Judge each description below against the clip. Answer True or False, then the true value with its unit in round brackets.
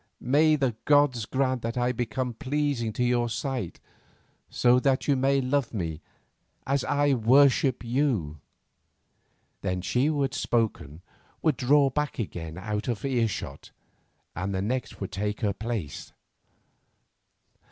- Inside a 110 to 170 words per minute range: True (140 wpm)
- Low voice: True (125 Hz)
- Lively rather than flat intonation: False (4.4 semitones)